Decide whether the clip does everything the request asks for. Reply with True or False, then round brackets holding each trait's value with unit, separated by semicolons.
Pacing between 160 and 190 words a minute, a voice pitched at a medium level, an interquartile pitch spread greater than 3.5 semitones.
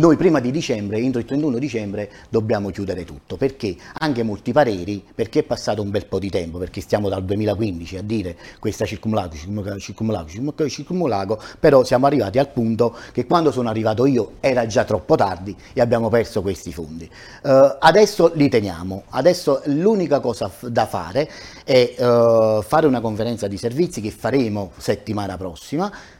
False (165 wpm; 115 Hz; 4.7 semitones)